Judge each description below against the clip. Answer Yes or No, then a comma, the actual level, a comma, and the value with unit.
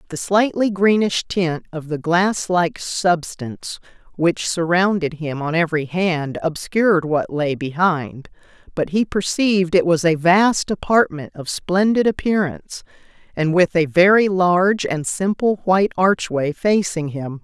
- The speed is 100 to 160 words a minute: Yes, average, 140 wpm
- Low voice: No, medium, 175 Hz